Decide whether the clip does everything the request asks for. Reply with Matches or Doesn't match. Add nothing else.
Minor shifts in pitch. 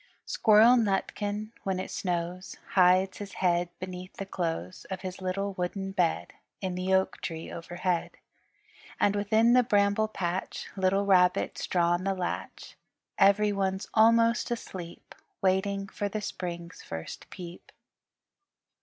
Matches